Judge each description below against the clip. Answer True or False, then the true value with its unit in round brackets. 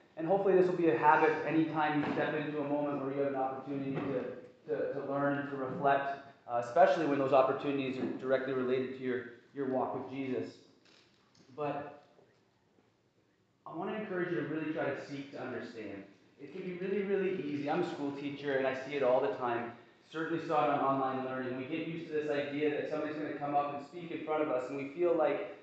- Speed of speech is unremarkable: False (225 wpm)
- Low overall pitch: False (145 Hz)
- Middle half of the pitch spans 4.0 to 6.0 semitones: False (2.8 semitones)